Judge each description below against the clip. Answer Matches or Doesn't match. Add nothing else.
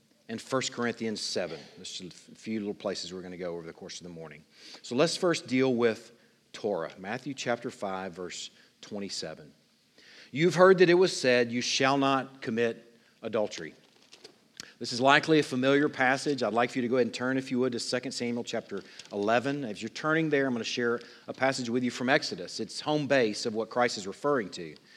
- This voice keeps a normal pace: Doesn't match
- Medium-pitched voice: Doesn't match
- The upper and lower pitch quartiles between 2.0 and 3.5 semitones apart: Matches